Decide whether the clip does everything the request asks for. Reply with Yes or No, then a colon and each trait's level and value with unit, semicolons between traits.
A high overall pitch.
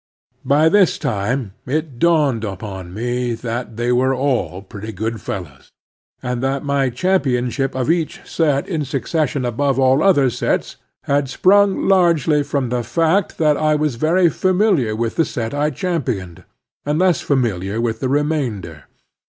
No: low, 135 Hz